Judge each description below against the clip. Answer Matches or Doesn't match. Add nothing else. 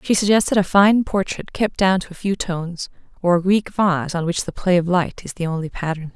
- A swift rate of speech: Matches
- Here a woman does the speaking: Matches